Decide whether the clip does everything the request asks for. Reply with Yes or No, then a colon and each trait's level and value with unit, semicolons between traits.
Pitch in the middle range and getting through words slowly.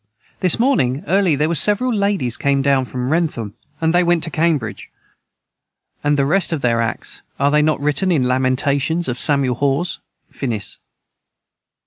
No: medium, 145 Hz; average, 165 wpm